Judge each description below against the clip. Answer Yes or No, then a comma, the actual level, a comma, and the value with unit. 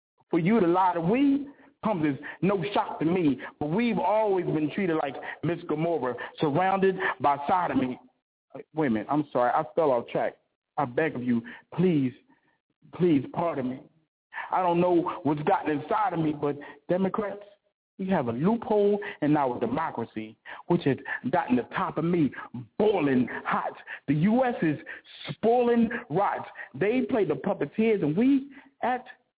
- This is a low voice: No, medium, 175 Hz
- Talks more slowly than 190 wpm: Yes, average, 160 wpm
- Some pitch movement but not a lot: No, wide, 6.3 semitones